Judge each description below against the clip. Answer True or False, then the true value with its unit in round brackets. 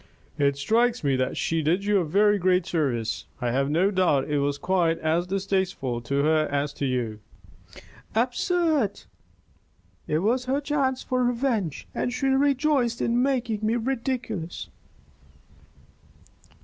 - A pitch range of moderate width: False (8.8 semitones)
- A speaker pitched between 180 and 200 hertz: True (190 Hz)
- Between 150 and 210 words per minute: False (140 wpm)